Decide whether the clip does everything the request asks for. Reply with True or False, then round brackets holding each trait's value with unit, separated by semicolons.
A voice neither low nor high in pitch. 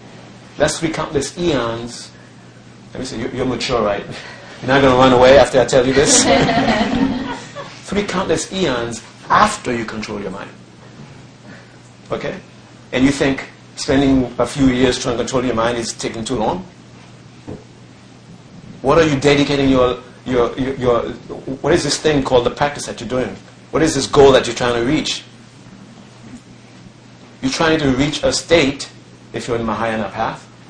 False (125 Hz)